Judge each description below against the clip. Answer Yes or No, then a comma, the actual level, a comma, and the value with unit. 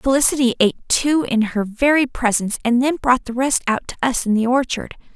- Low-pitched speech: No, very high, 250 Hz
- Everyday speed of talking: No, fast, 210 wpm